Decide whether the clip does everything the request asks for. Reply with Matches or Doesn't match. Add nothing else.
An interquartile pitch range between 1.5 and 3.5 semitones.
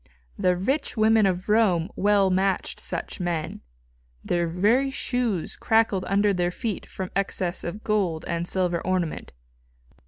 Matches